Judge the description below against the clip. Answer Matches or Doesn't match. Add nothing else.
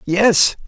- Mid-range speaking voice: Doesn't match